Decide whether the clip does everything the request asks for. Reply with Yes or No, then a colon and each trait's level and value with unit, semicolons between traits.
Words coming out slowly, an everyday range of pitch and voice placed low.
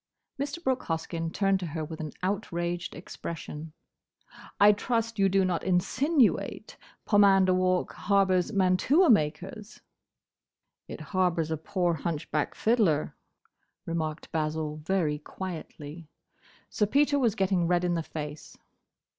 No: slow, 120 wpm; average, 4.0 semitones; medium, 180 Hz